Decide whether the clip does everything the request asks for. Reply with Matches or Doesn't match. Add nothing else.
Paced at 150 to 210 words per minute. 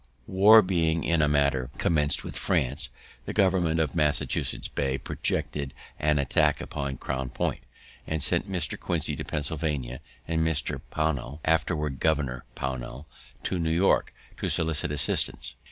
Doesn't match